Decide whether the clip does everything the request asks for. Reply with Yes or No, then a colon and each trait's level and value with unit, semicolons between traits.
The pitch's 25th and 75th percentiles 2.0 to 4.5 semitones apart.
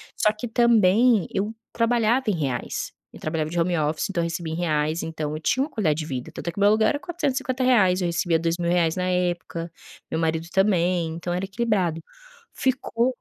No: average, 5.3 semitones